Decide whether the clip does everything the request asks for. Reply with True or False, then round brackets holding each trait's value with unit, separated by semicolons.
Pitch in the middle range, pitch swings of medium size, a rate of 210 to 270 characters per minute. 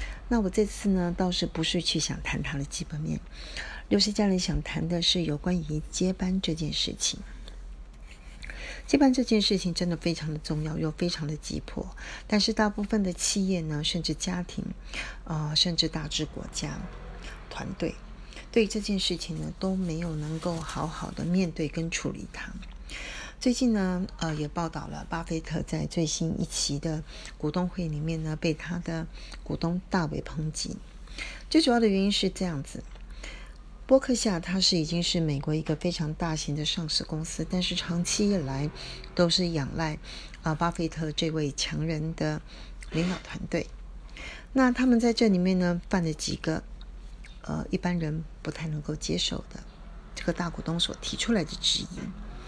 True (170 Hz; 3.1 semitones; 250 characters per minute)